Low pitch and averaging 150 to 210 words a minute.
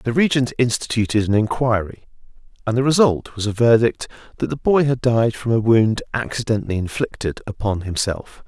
Yes: low, 115 Hz; average, 165 wpm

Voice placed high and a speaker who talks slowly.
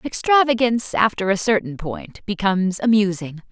Yes: high, 205 Hz; slow, 120 wpm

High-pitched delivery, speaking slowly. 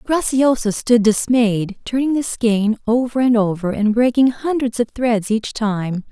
No: high, 230 Hz; average, 155 wpm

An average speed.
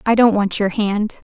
No: fast, 230 wpm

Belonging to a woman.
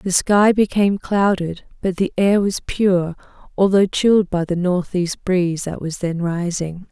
Yes: female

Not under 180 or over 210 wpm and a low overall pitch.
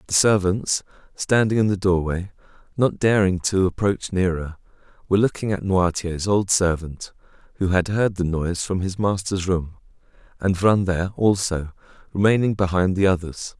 No: average, 150 wpm; very low, 95 Hz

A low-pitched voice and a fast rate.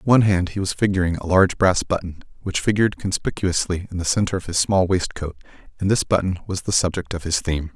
Yes: very low, 90 Hz; fast, 225 wpm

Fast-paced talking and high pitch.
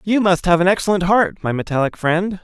No: fast, 220 wpm; medium, 175 Hz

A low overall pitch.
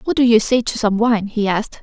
No: high, 225 Hz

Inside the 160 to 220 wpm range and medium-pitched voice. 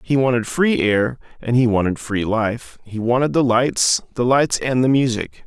No: average, 200 wpm; low, 120 Hz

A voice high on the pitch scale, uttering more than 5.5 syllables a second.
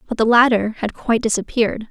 Yes: high, 225 Hz; 6.4 syllables/s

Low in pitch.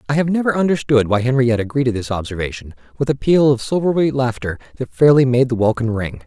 Yes: low, 125 Hz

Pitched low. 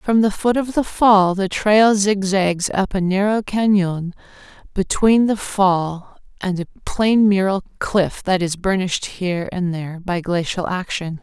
No: high, 190 Hz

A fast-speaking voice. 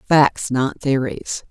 No: slow, 120 wpm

